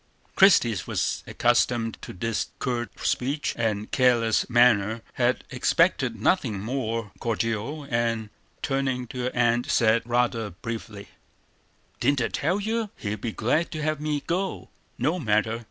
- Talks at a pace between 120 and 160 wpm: Yes, average, 140 wpm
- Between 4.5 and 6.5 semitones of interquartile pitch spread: No, average, 3.5 semitones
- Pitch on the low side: Yes, low, 120 Hz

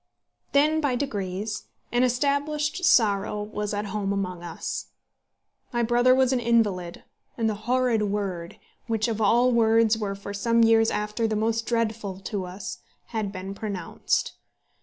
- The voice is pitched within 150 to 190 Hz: No, high, 220 Hz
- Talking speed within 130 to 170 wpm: Yes, average, 150 wpm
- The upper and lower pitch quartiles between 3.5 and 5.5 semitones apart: No, average, 3.1 semitones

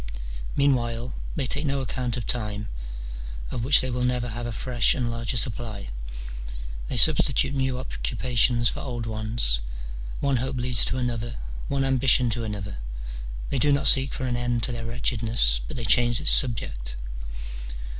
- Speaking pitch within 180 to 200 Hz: No, low, 120 Hz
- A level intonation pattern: Yes, narrow, 2.2 semitones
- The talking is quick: No, average, 165 wpm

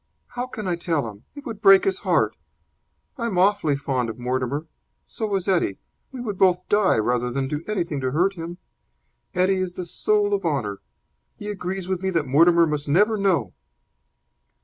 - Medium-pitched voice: Yes, medium, 175 Hz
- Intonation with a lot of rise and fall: Yes, wide, 5.8 semitones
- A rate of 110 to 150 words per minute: No, average, 185 wpm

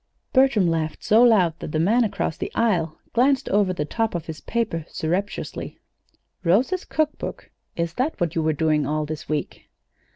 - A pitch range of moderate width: No, wide, 6.5 semitones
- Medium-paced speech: Yes, average, 175 wpm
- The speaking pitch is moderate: Yes, medium, 175 Hz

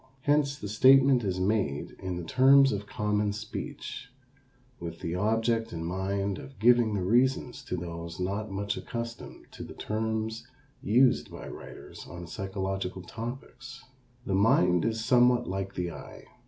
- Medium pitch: No, low, 105 Hz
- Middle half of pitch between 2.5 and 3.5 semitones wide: No, average, 4.4 semitones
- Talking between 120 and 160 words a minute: Yes, average, 150 wpm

